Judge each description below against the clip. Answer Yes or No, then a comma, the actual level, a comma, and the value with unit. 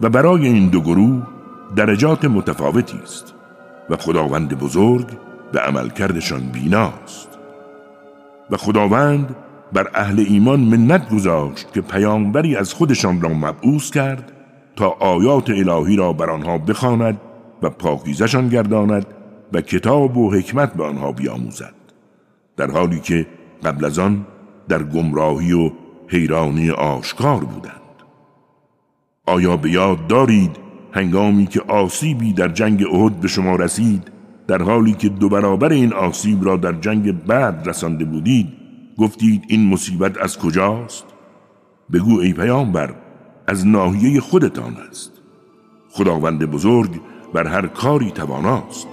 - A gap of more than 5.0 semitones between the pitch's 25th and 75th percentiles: Yes, wide, 5.4 semitones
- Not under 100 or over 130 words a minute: Yes, average, 125 wpm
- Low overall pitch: Yes, low, 100 Hz